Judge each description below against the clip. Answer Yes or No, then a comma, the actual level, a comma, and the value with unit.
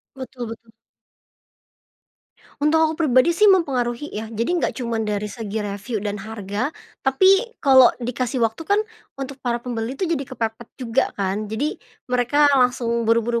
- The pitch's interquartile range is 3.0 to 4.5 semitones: Yes, average, 3.6 semitones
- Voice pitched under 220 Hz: No, high, 245 Hz